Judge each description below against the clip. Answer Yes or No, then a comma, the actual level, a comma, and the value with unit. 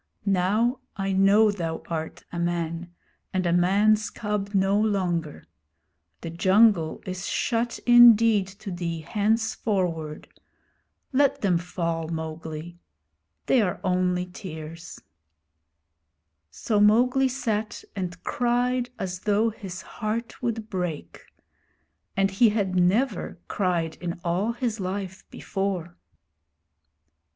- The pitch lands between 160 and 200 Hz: Yes, high, 190 Hz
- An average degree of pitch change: Yes, average, 3.8 semitones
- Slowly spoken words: Yes, slow, 110 wpm